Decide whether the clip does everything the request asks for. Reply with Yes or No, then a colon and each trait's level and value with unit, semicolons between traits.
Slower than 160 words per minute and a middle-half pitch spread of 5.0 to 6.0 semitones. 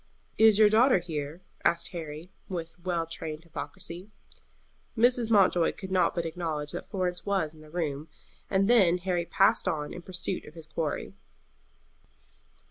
No: average, 150 wpm; average, 3.2 semitones